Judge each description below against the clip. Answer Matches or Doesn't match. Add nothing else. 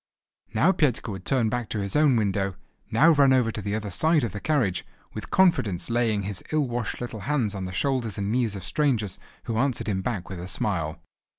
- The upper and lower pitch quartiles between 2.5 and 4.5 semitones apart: Doesn't match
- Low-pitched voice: Matches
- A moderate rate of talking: Doesn't match